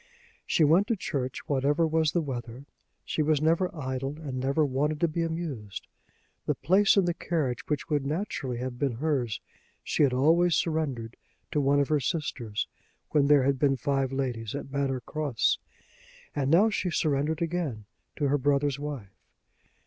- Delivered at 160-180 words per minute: Yes, average, 170 wpm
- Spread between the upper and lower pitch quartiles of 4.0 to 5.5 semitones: No, average, 3.4 semitones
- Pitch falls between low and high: Yes, medium, 145 Hz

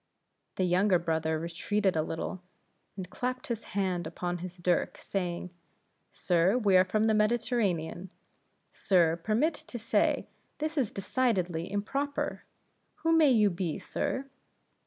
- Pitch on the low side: No, high, 190 Hz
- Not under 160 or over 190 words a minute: No, slow, 135 wpm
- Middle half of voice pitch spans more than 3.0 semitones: Yes, average, 4.7 semitones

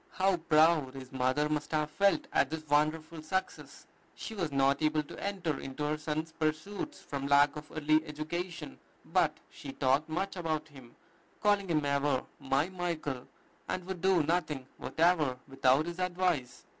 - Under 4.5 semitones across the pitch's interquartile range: Yes, average, 3.3 semitones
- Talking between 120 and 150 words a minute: No, average, 160 wpm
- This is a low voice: No, medium, 155 Hz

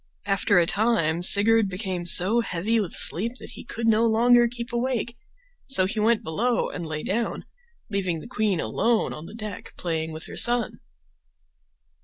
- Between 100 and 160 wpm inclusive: No, average, 170 wpm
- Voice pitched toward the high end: Yes, high, 215 Hz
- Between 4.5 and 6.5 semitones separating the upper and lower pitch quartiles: Yes, average, 4.8 semitones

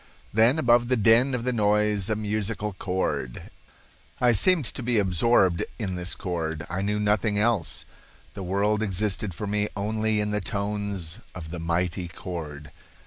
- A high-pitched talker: No, low, 105 Hz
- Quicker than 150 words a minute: Yes, average, 160 wpm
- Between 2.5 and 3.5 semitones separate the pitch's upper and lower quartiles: Yes, average, 3.2 semitones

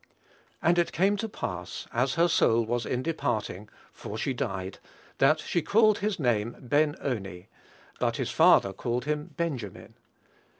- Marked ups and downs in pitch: Yes, wide, 7.6 semitones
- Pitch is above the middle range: No, low, 125 Hz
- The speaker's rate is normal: Yes, average, 155 wpm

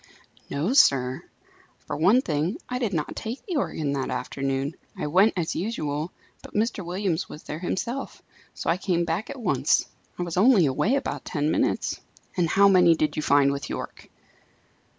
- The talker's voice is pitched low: No, medium, 170 Hz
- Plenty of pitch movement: Yes, wide, 5.9 semitones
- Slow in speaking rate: No, average, 175 wpm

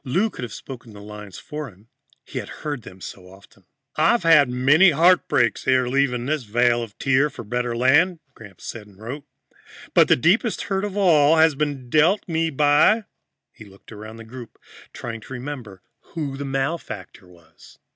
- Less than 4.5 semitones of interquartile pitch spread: No, wide, 5.6 semitones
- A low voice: Yes, low, 130 Hz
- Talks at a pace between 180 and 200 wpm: Yes, average, 190 wpm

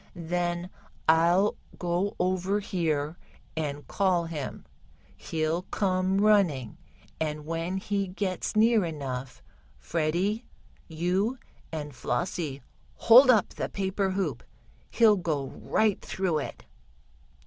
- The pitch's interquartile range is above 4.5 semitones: No, average, 3.8 semitones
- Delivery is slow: Yes, slow, 105 wpm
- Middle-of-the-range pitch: Yes, medium, 175 Hz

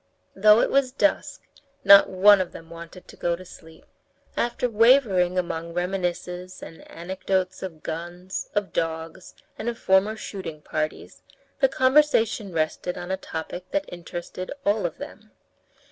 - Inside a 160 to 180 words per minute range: No, average, 145 wpm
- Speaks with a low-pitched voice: No, medium, 185 Hz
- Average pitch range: Yes, average, 3.6 semitones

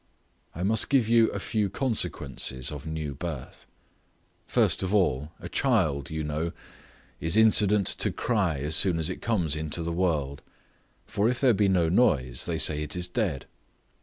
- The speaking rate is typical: Yes, average, 170 wpm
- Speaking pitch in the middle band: No, very low, 85 Hz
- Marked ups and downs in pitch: Yes, wide, 5.7 semitones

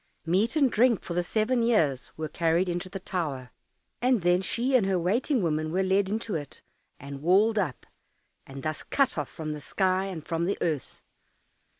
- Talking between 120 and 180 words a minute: No, average, 190 wpm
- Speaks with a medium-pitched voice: Yes, medium, 180 Hz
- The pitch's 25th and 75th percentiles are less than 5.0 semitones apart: No, wide, 5.4 semitones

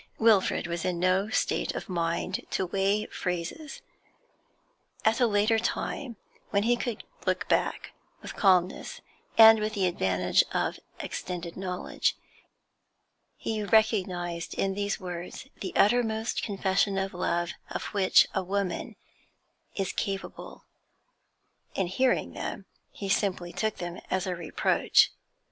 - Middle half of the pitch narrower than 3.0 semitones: No, average, 3.3 semitones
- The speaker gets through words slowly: Yes, slow, 125 wpm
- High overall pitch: Yes, high, 195 Hz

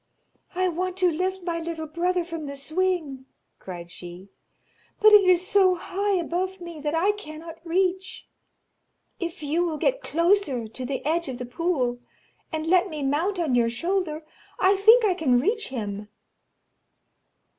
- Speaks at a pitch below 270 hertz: No, very high, 335 Hz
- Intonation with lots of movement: No, average, 4.5 semitones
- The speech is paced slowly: No, average, 160 wpm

